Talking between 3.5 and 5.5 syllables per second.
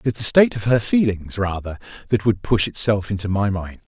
No: 5.8 syllables/s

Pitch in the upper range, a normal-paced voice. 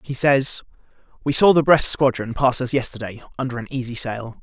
No: low, 130 Hz; average, 175 wpm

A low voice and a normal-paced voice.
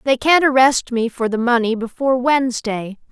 No: high, 245 Hz; average, 175 wpm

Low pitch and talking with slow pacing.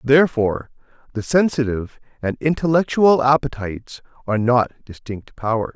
Yes: low, 130 Hz; slow, 105 wpm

